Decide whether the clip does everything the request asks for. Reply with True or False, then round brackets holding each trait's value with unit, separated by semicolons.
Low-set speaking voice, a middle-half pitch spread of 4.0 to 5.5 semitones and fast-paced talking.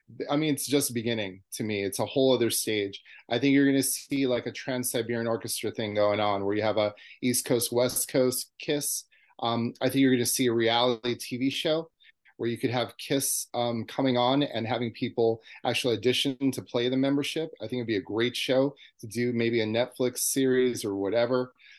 False (125 Hz; 2.4 semitones; 215 wpm)